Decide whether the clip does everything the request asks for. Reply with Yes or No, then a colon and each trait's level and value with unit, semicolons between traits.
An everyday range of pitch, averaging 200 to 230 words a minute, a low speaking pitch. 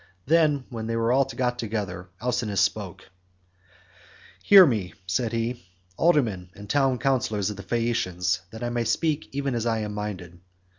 No: average, 3.8 semitones; average, 155 wpm; low, 115 Hz